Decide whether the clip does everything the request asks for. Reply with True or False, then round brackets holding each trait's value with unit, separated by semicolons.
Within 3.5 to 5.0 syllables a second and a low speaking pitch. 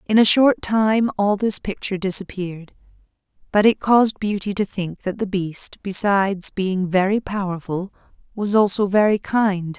False (4.7 syllables/s; 200 Hz)